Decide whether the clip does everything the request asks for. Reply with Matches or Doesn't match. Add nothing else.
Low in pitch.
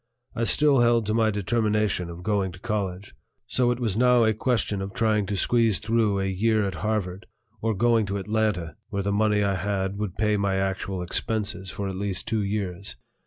Matches